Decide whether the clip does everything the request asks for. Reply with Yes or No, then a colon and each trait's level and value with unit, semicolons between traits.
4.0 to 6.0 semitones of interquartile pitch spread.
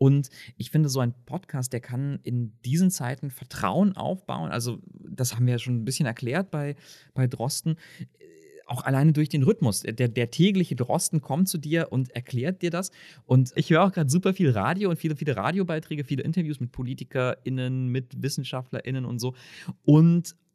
Yes: average, 4.7 semitones